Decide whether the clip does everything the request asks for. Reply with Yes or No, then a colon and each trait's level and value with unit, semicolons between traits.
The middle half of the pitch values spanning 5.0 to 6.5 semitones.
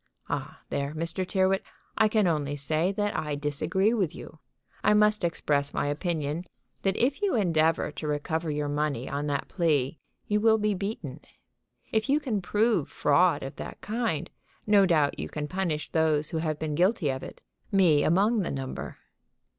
Yes: wide, 5.6 semitones